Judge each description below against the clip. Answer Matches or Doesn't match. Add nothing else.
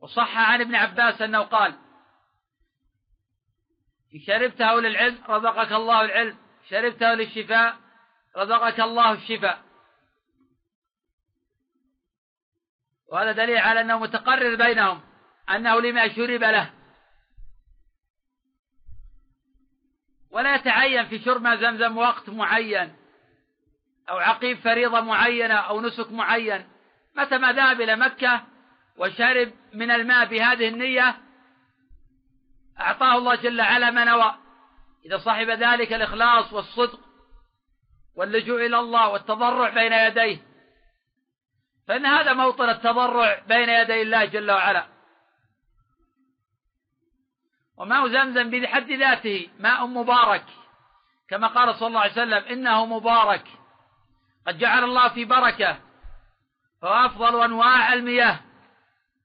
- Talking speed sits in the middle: Matches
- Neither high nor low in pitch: Doesn't match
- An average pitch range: Doesn't match